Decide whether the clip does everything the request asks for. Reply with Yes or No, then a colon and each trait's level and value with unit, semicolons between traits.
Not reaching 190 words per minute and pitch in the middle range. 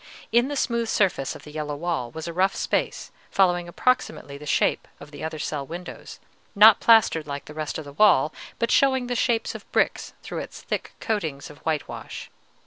No: average, 195 wpm; medium, 170 Hz